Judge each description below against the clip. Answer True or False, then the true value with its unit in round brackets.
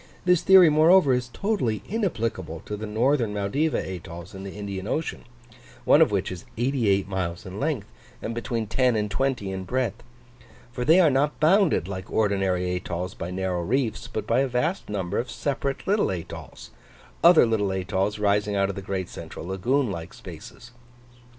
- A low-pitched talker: True (110 Hz)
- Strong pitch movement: True (6.0 semitones)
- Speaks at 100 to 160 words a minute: False (175 wpm)